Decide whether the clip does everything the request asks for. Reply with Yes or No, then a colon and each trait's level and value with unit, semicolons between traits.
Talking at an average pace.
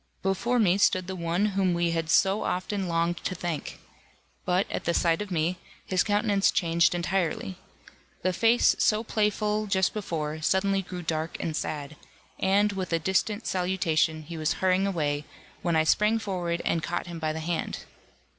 Yes: average, 170 wpm